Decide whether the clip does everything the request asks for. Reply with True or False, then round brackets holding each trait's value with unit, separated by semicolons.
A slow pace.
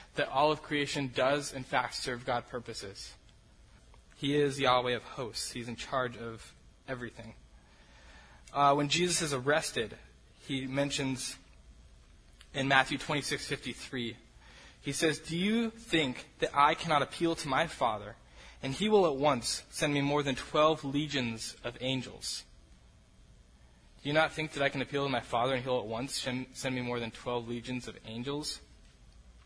False (165 wpm)